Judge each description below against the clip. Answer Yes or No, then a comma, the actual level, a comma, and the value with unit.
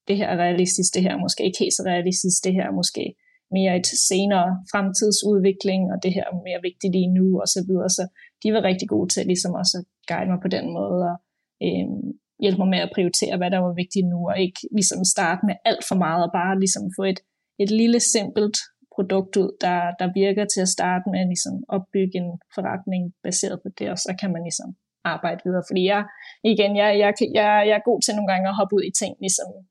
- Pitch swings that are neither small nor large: No, narrow, 1.9 semitones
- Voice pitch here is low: No, high, 190 Hz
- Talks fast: Yes, fast, 230 wpm